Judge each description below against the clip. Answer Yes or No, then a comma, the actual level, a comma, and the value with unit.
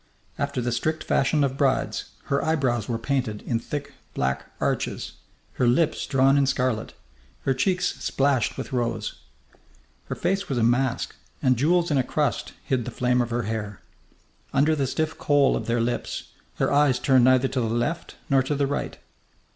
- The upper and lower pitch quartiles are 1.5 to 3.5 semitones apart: Yes, average, 3.1 semitones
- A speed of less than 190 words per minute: Yes, average, 180 wpm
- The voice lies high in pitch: No, low, 130 Hz